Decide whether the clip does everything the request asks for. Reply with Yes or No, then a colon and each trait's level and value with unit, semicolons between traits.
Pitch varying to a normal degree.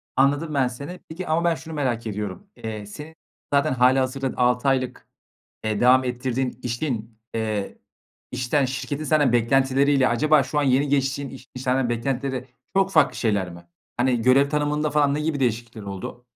Yes: average, 3.0 semitones